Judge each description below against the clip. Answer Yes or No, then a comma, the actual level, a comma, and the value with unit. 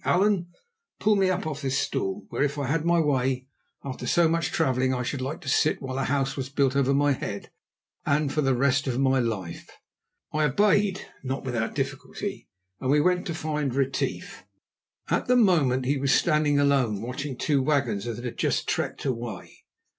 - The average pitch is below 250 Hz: Yes, medium, 140 Hz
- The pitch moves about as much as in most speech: Yes, average, 3.0 semitones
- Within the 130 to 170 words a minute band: No, average, 190 wpm